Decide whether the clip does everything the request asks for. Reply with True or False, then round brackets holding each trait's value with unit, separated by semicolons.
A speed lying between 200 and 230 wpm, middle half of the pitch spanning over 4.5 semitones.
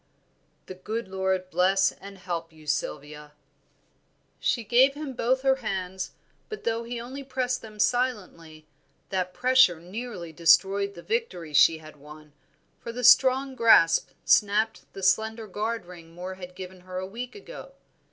False (150 wpm; 5.1 semitones)